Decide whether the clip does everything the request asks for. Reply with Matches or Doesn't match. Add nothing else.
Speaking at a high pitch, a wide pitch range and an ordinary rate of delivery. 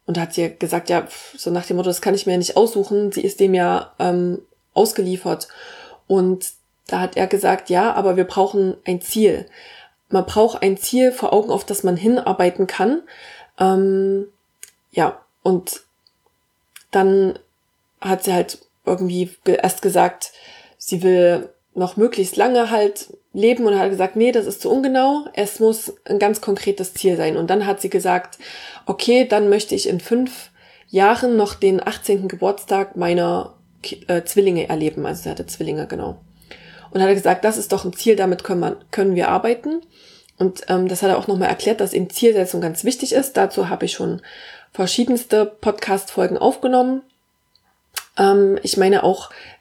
Doesn't match